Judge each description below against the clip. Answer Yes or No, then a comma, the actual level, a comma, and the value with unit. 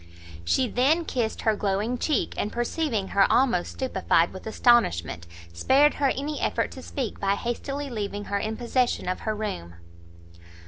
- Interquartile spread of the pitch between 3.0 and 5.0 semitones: Yes, average, 4.7 semitones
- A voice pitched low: No, high, 225 Hz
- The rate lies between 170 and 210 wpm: No, average, 155 wpm